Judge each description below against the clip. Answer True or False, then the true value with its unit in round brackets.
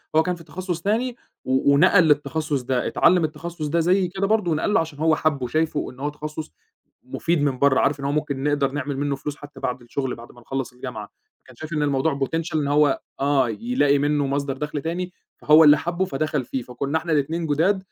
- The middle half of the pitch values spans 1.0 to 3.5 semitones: True (3.0 semitones)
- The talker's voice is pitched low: False (150 Hz)